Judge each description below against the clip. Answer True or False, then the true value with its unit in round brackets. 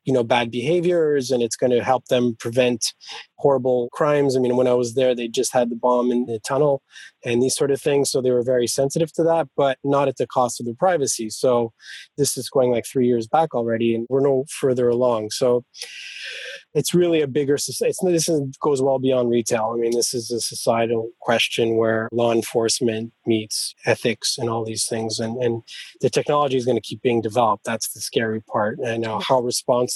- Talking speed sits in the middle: False (215 wpm)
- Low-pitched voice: True (125 Hz)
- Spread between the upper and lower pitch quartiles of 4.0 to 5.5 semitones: False (2.7 semitones)